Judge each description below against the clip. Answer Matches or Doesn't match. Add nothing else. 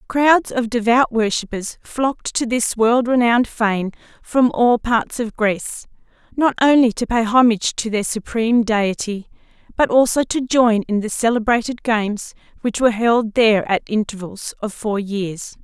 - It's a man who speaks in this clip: Doesn't match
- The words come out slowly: Doesn't match